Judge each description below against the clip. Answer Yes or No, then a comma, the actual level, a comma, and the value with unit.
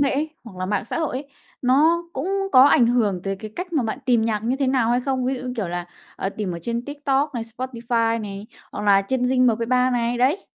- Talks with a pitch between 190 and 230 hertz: No, high, 245 Hz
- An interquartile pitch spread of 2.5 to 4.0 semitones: Yes, average, 3.2 semitones